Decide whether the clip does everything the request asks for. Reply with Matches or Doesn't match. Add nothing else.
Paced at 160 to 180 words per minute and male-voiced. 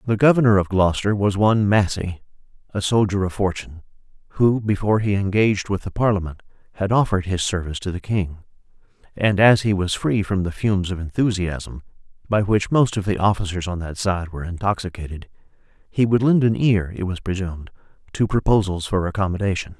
Matches